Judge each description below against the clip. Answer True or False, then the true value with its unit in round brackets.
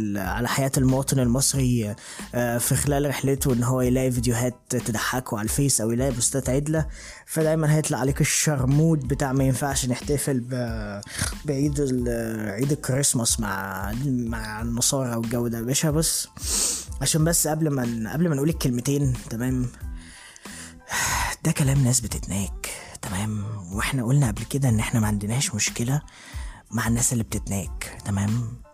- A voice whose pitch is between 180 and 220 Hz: False (125 Hz)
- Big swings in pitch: False (3.8 semitones)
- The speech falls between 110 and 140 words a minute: True (135 wpm)